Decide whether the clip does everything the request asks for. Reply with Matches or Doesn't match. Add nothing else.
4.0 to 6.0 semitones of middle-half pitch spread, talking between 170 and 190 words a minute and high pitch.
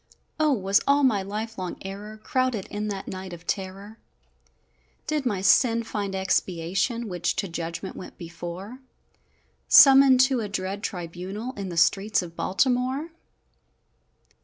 Doesn't match